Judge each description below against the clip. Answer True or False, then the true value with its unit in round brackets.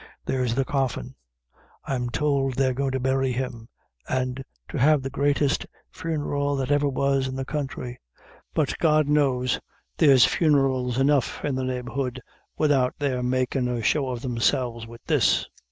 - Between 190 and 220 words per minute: False (155 wpm)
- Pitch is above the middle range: False (130 Hz)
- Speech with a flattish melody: True (1.9 semitones)